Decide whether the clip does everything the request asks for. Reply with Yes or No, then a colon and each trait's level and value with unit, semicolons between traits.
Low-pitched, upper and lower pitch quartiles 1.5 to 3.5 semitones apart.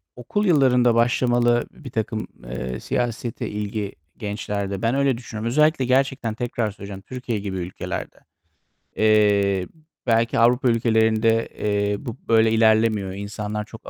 Yes: low, 110 Hz; average, 2.9 semitones